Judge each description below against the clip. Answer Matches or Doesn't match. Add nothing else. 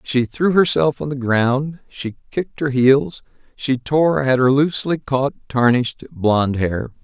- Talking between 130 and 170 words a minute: Matches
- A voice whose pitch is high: Doesn't match